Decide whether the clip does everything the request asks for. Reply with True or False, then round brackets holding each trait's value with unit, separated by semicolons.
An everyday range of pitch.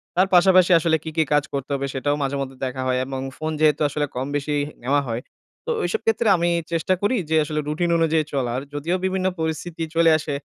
True (3.7 semitones)